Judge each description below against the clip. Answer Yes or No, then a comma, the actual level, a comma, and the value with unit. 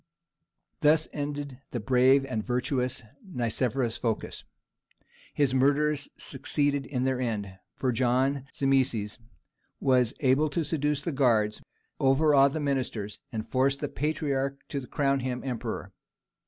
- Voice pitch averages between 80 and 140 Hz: Yes, low, 135 Hz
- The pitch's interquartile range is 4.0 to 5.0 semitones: No, narrow, 2.4 semitones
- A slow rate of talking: Yes, slow, 125 wpm